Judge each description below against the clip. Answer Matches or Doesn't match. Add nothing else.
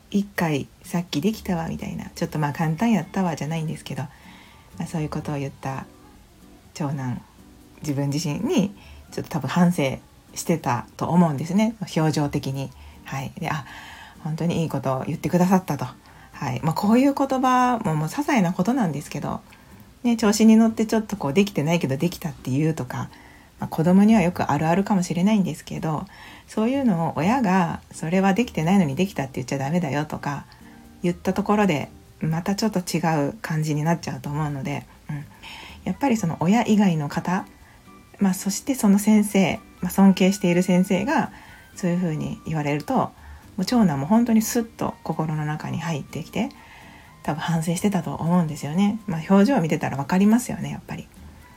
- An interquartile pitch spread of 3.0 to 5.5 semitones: Matches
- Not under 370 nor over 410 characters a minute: Matches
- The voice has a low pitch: Doesn't match